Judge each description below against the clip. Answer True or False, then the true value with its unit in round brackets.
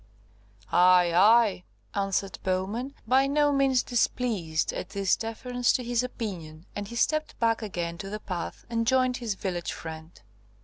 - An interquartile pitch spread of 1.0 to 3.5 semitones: False (5.3 semitones)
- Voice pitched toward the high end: True (215 Hz)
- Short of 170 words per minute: True (150 wpm)